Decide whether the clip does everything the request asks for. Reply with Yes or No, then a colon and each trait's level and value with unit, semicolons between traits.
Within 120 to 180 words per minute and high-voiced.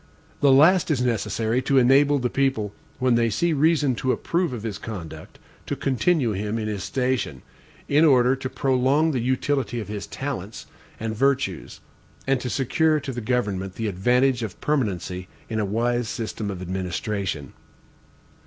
No: average, 160 wpm; low, 125 Hz